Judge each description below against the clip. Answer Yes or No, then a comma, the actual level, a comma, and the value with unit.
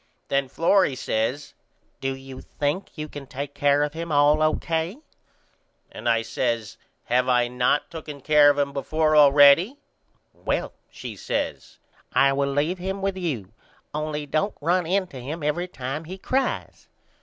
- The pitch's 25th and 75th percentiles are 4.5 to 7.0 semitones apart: No, average, 3.3 semitones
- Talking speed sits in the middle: Yes, average, 155 wpm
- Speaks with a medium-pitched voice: Yes, medium, 145 Hz